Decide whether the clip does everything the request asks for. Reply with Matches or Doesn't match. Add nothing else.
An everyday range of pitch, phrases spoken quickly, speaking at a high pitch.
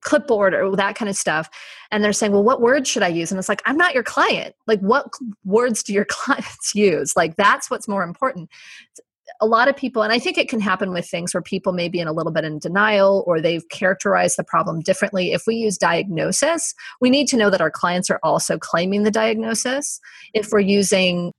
Matches